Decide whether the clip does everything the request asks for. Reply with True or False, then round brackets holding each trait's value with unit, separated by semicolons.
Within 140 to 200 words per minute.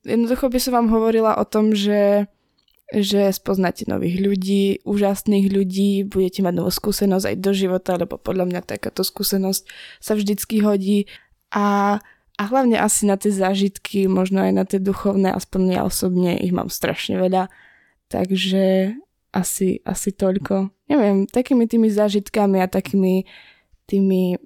True (145 wpm)